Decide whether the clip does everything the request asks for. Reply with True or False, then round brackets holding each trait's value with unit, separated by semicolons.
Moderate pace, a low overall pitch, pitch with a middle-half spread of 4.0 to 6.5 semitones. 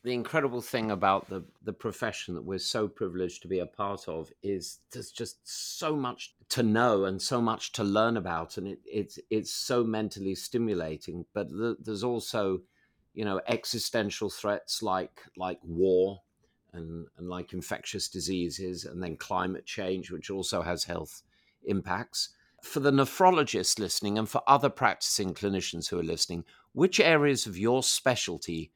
True (165 wpm; 100 Hz; 4.6 semitones)